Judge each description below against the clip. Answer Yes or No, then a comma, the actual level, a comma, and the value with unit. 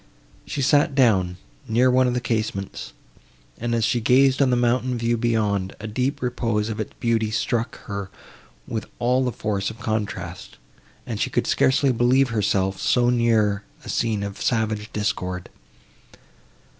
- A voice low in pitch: Yes, low, 115 Hz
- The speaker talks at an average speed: Yes, average, 155 wpm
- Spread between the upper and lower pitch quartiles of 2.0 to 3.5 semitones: Yes, average, 2.9 semitones